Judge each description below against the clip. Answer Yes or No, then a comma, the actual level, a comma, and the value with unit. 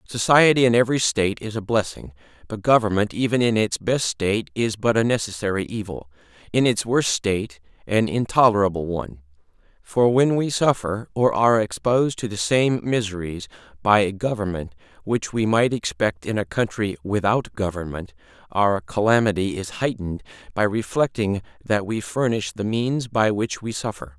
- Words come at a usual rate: Yes, average, 160 wpm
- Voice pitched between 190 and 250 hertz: No, low, 105 Hz